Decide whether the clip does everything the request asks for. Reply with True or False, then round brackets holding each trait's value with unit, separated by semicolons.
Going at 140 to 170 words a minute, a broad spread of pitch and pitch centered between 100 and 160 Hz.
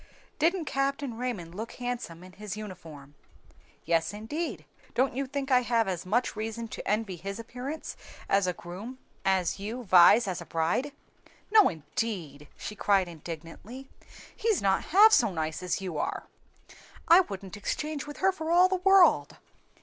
False (160 wpm; 7.1 semitones; 215 Hz)